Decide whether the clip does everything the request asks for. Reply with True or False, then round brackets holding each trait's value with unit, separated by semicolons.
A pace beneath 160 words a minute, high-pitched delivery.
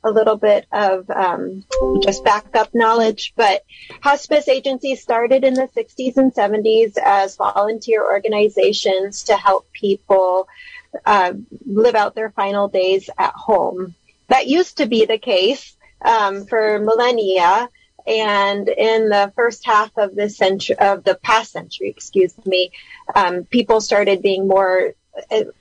True (140 wpm; 215 Hz)